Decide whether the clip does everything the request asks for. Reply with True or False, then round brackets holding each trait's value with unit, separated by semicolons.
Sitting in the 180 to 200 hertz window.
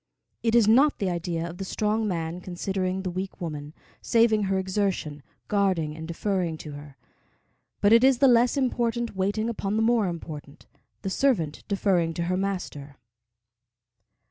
True (190 Hz)